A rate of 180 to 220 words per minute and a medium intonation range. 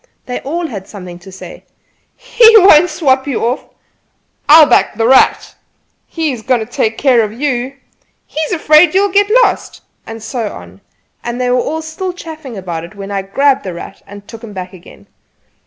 No: average, 190 wpm; wide, 7.4 semitones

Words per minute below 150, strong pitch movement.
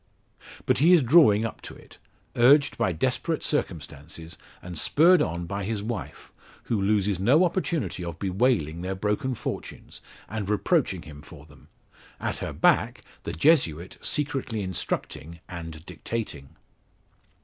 Yes: average, 140 wpm; wide, 7.3 semitones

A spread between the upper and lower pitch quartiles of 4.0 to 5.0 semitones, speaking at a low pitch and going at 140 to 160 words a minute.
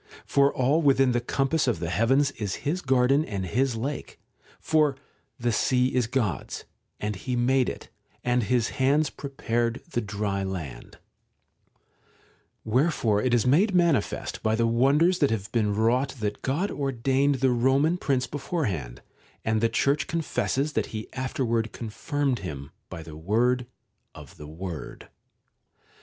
Yes: average, 4.3 semitones; low, 125 Hz; average, 150 wpm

